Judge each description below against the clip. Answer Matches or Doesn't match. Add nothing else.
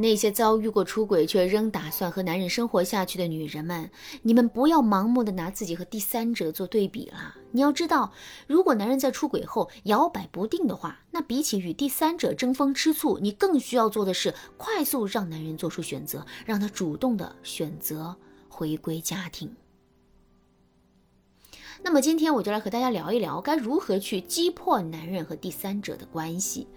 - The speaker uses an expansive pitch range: Matches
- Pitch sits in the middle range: Doesn't match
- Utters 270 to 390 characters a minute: Matches